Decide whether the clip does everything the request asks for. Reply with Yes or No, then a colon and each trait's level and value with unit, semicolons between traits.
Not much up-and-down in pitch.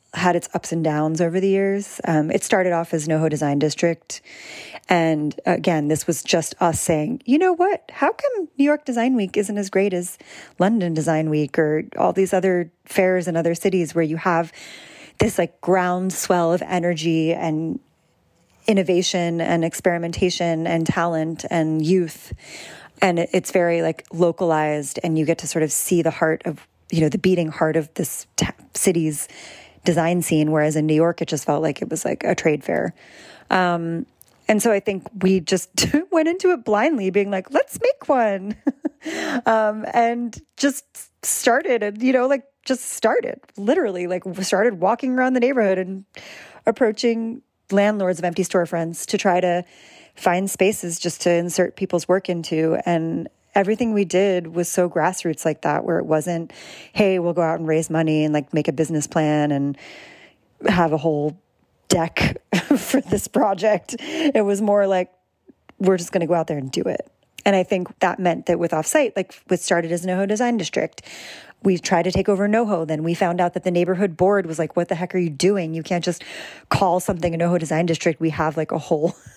No: average, 3.5 semitones